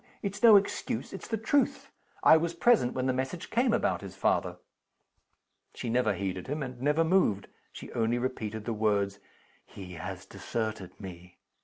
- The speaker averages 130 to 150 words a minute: No, average, 165 wpm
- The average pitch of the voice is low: Yes, low, 120 Hz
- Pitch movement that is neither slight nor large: No, wide, 8.7 semitones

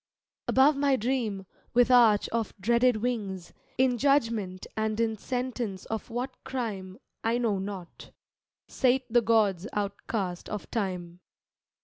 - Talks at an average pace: No, slow, 125 wpm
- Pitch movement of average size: Yes, average, 3.9 semitones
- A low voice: No, high, 225 Hz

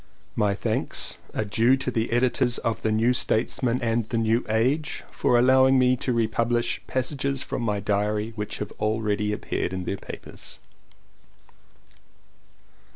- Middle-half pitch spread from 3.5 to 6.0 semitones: No, average, 2.9 semitones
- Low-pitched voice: Yes, low, 115 Hz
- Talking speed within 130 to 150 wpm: Yes, average, 145 wpm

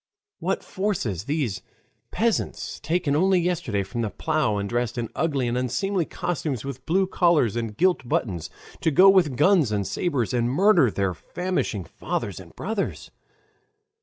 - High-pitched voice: No, medium, 140 Hz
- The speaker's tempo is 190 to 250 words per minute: No, average, 155 wpm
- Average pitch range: No, wide, 7.9 semitones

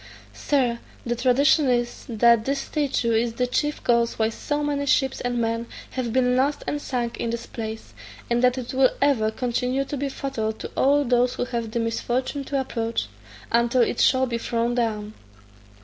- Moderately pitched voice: No, high, 245 Hz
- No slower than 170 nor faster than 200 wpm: Yes, average, 185 wpm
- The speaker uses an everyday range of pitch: No, narrow, 2.3 semitones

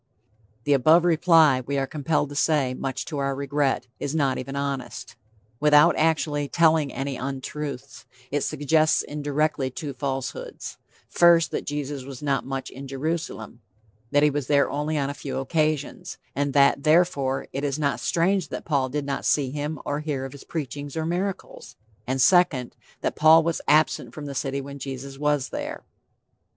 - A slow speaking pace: No, average, 170 wpm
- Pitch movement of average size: No, narrow, 2.3 semitones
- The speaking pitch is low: No, medium, 145 Hz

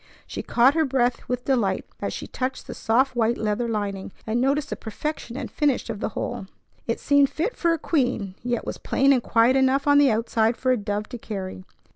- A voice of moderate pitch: No, high, 245 Hz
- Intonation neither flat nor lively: Yes, average, 3.7 semitones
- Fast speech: Yes, fast, 215 wpm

